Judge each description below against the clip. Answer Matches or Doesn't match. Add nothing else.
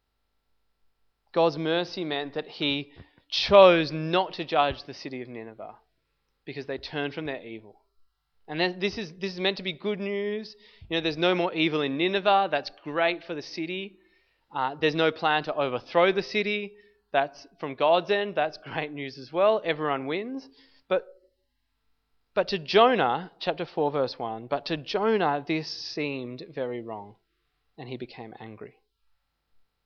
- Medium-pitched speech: Matches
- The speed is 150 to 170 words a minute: Matches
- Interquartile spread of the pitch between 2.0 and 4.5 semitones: Doesn't match